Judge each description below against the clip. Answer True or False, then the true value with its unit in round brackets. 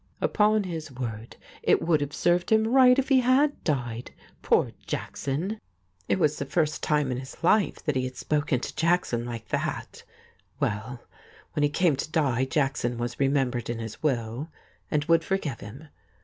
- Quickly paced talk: False (170 wpm)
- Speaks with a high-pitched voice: False (145 Hz)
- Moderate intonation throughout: False (5.7 semitones)